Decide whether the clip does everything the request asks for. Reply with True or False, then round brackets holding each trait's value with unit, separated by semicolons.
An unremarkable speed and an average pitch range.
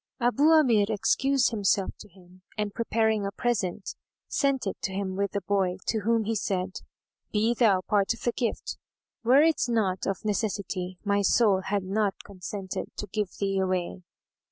True (170 wpm; 3.0 semitones)